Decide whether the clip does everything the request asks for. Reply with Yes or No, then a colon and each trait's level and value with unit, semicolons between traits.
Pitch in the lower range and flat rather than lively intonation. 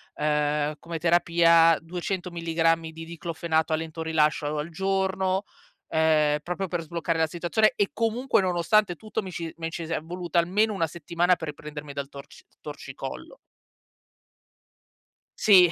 No: medium, 170 Hz; narrow, 2.2 semitones